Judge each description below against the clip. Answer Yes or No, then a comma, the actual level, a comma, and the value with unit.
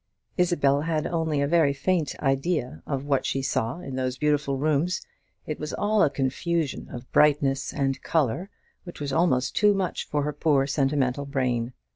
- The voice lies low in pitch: No, medium, 145 Hz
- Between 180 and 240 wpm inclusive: No, average, 170 wpm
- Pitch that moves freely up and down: No, average, 3.2 semitones